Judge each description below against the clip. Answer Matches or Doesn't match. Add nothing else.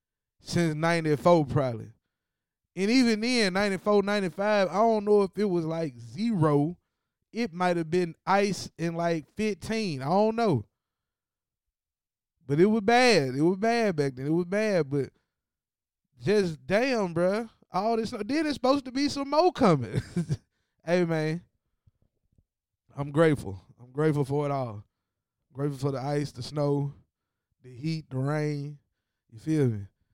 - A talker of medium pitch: Matches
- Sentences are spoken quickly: Doesn't match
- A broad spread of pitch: Matches